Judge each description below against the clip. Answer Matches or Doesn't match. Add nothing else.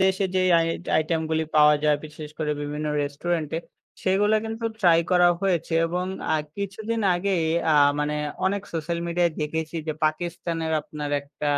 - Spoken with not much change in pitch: Doesn't match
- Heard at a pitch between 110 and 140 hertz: Doesn't match